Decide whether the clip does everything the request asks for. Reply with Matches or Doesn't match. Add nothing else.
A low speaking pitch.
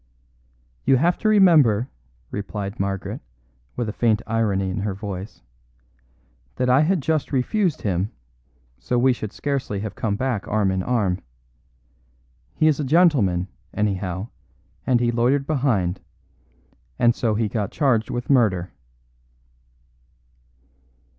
Matches